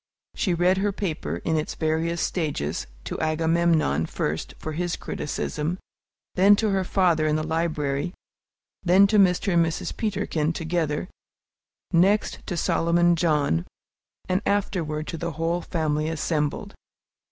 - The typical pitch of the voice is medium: Yes, medium, 165 Hz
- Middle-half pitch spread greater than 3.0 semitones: No, narrow, 2.6 semitones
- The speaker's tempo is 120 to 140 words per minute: Yes, slow, 135 wpm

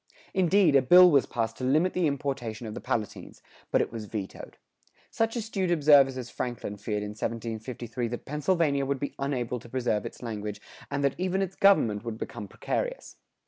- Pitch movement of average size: No, wide, 6.0 semitones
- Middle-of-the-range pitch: No, low, 130 Hz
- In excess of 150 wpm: Yes, average, 185 wpm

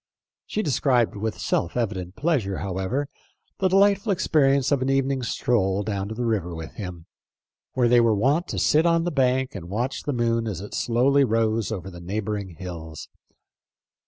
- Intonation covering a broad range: Yes, wide, 5.8 semitones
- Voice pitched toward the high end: No, low, 115 Hz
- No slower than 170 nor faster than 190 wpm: Yes, average, 175 wpm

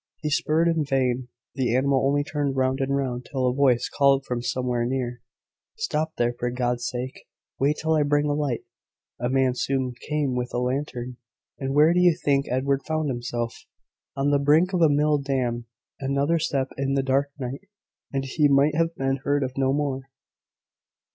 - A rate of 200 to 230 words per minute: No, average, 185 wpm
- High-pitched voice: No, low, 135 Hz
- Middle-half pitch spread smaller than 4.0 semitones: Yes, narrow, 2.4 semitones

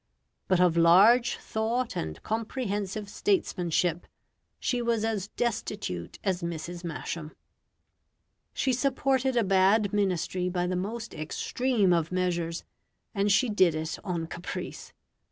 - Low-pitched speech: No, high, 195 Hz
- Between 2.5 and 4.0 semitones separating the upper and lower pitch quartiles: No, average, 4.6 semitones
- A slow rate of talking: Yes, slow, 120 wpm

